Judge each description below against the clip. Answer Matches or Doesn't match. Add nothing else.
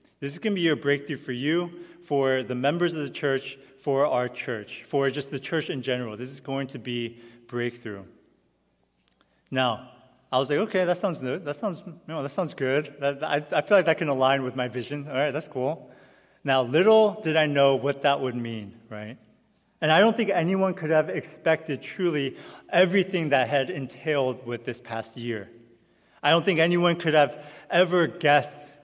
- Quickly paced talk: Doesn't match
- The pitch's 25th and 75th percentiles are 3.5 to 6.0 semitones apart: Matches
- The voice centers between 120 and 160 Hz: Matches